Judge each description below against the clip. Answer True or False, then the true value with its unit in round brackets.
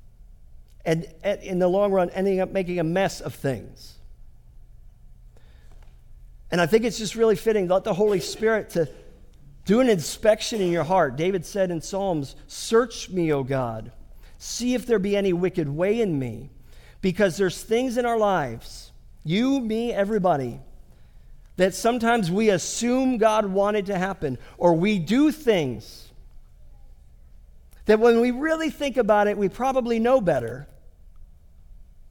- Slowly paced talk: False (150 wpm)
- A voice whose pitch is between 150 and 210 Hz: True (190 Hz)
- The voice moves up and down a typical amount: False (8.4 semitones)